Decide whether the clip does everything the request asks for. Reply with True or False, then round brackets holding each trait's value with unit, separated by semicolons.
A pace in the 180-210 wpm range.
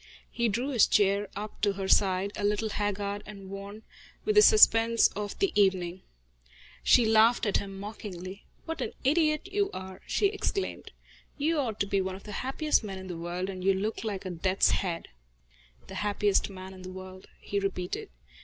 True (190 wpm)